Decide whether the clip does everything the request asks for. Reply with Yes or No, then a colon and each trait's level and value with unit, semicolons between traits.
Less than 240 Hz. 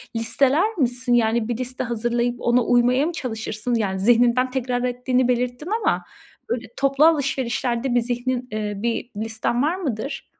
No: high, 245 Hz